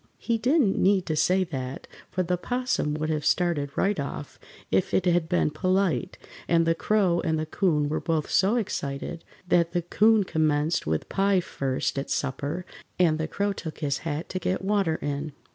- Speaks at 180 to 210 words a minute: Yes, average, 185 wpm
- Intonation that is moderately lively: Yes, average, 4.0 semitones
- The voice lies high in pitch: No, medium, 170 Hz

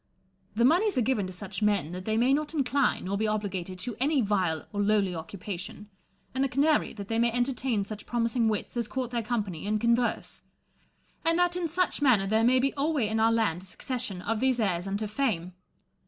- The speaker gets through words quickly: Yes, fast, 210 wpm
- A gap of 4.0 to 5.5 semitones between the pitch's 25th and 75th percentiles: Yes, average, 4.4 semitones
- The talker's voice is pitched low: No, high, 225 Hz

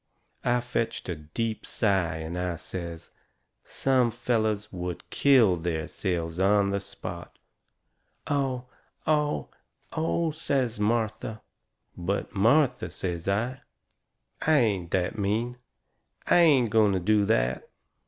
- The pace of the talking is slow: Yes, slow, 120 wpm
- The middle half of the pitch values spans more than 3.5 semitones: Yes, wide, 5.5 semitones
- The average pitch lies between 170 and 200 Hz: No, low, 105 Hz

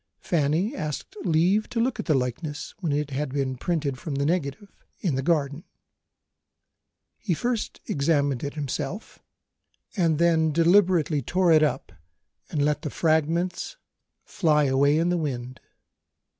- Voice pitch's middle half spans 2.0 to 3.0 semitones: No, average, 3.5 semitones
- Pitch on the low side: No, medium, 155 Hz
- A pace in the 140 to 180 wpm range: Yes, average, 145 wpm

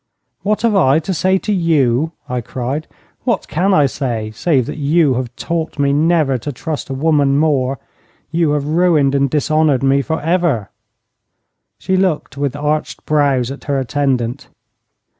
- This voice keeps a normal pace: Yes, average, 160 wpm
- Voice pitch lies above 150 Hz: No, medium, 145 Hz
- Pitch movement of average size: Yes, average, 3.3 semitones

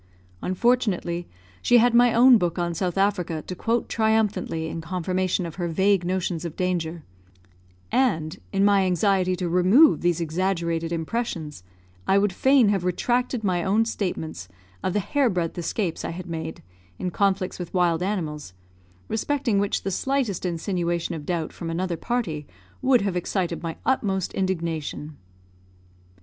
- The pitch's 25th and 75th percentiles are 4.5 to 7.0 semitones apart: No, average, 3.4 semitones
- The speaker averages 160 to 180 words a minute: No, average, 150 wpm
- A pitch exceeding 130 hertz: Yes, medium, 185 Hz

